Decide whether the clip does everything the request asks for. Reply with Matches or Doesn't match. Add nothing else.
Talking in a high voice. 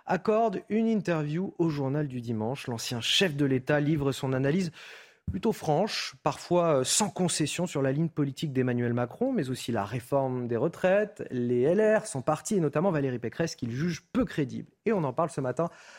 Doesn't match